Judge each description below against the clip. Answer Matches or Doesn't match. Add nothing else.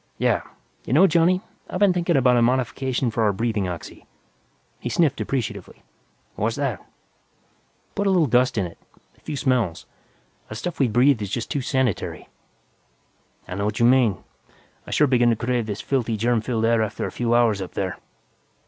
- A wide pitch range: Doesn't match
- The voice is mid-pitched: Doesn't match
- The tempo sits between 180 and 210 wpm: Matches